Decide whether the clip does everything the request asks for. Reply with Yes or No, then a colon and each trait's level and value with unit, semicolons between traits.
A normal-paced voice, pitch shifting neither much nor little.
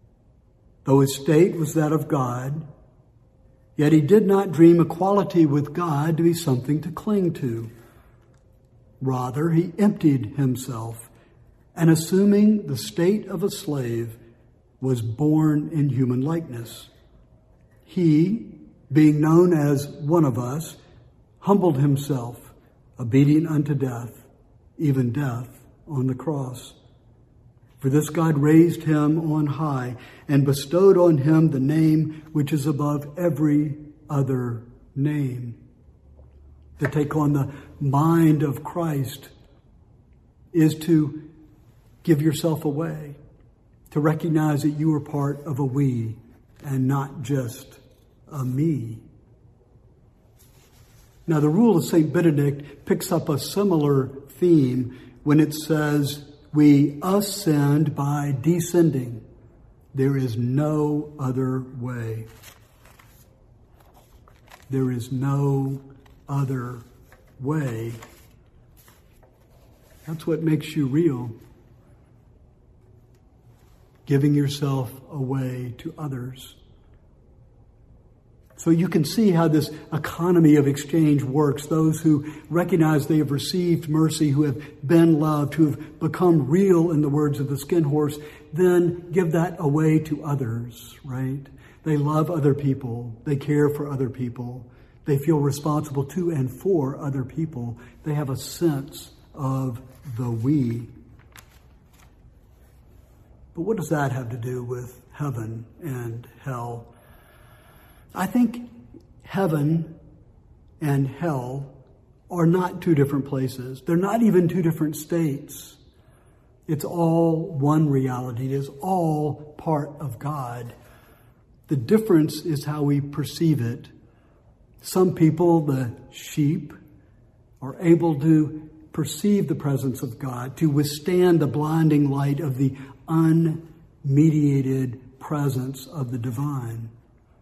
No: slow, 115 wpm; average, 3.9 semitones